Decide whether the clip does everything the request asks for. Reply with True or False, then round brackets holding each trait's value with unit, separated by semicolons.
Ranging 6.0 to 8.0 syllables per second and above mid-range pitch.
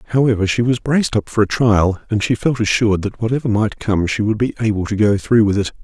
False (6.2 syllables/s; 110 Hz)